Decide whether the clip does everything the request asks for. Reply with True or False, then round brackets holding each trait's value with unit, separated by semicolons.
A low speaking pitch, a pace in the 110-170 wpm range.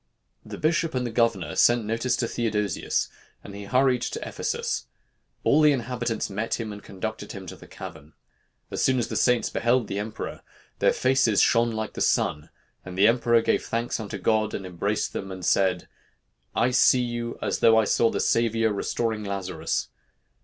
False (115 Hz; 180 wpm)